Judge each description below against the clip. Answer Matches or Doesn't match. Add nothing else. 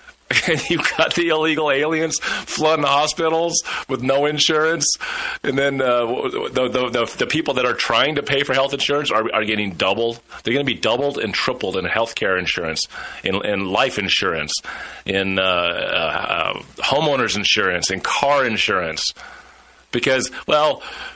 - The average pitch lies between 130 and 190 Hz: Matches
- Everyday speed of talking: Matches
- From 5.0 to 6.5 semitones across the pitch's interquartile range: Matches